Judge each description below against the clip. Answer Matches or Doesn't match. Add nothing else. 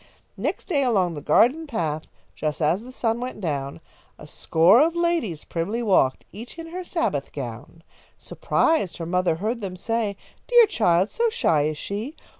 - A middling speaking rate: Matches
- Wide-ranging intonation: Matches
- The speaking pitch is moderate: Doesn't match